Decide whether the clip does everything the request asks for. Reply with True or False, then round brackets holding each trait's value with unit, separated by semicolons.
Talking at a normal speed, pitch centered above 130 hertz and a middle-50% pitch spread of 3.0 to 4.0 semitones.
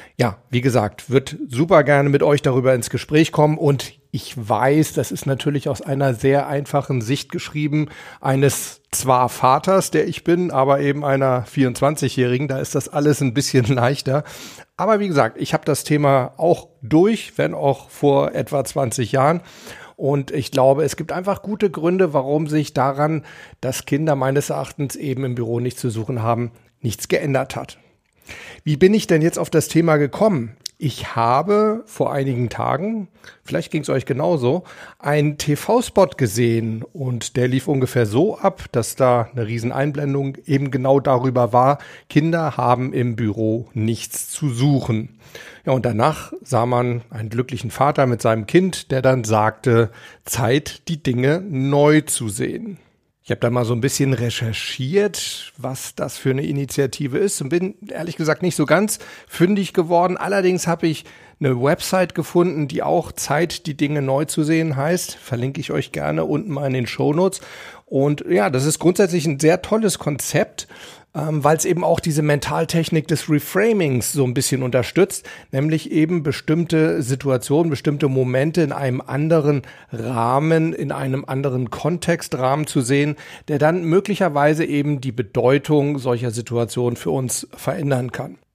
True (165 wpm; 140 Hz; 3.7 semitones)